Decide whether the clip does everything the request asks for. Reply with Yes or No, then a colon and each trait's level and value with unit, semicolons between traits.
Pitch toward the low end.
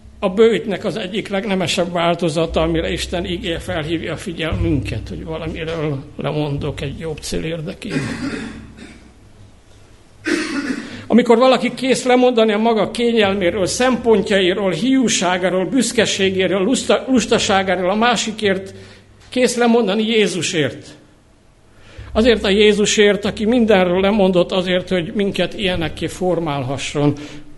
No: medium, 185 Hz